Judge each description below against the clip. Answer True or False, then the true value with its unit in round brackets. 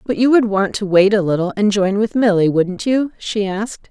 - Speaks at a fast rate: True (245 wpm)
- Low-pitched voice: False (205 Hz)